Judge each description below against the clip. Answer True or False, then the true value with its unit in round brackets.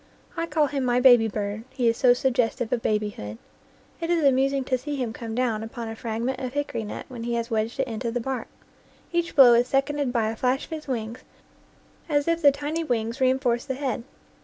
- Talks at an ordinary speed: False (215 wpm)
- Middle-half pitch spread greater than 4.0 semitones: False (3.1 semitones)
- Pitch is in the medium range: False (250 Hz)